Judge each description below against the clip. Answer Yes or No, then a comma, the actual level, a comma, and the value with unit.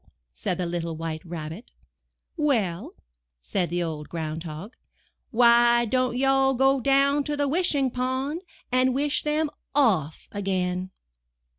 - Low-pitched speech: No, high, 235 Hz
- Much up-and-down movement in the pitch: Yes, wide, 7.9 semitones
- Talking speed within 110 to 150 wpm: Yes, slow, 135 wpm